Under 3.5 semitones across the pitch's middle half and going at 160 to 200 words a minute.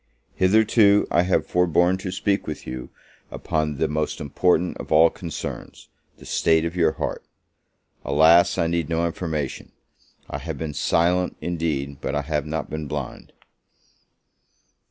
No: average, 2.9 semitones; average, 145 wpm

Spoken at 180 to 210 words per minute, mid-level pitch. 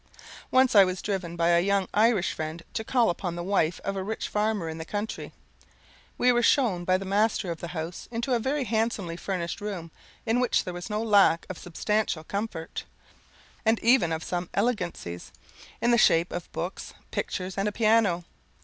No: average, 190 wpm; high, 195 Hz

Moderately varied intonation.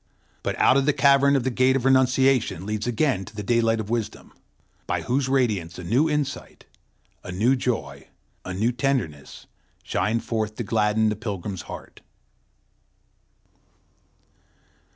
Yes: average, 4.1 semitones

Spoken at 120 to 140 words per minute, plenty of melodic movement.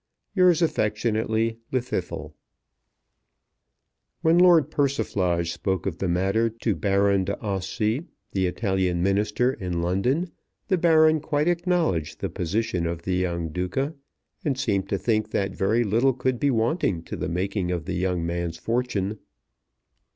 Yes: slow, 135 wpm; wide, 6.1 semitones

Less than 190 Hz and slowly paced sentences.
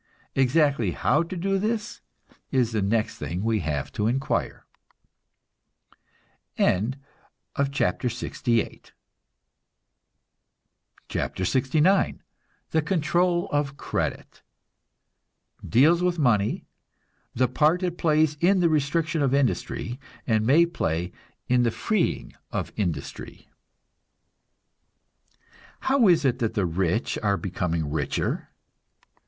Yes: low, 135 Hz; slow, 100 wpm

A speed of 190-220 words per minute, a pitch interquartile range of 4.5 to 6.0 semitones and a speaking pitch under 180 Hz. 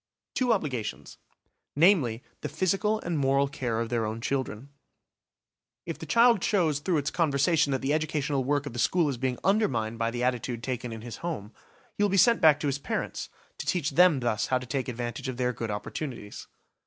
Yes: average, 200 wpm; average, 5.2 semitones; low, 135 Hz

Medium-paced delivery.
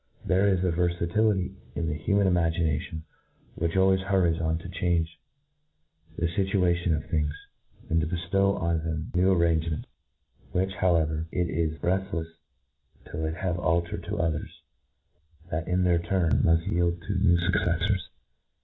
Yes: average, 145 wpm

